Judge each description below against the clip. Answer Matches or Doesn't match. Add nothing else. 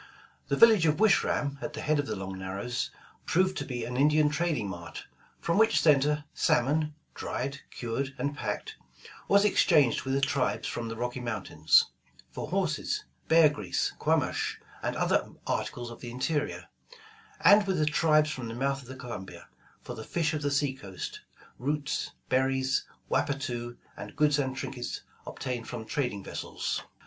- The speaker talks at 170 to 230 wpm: Matches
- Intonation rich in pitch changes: Doesn't match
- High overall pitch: Doesn't match